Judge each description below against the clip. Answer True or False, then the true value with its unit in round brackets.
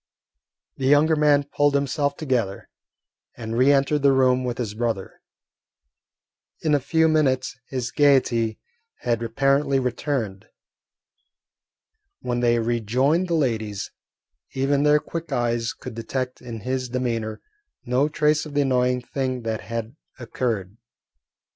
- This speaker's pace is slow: True (130 wpm)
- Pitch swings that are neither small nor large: True (3.5 semitones)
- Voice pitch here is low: True (130 Hz)